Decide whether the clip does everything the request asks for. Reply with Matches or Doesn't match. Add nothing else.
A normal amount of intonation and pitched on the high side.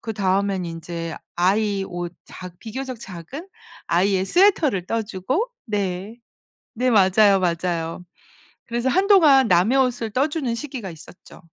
Doesn't match